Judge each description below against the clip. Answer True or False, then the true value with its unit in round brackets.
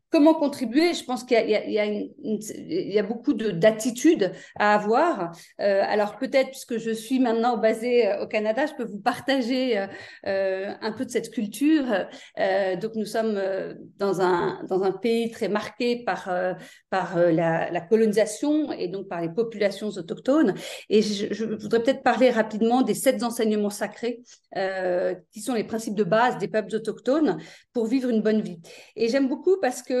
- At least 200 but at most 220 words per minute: False (185 wpm)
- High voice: True (220 Hz)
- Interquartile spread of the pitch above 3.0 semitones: True (3.6 semitones)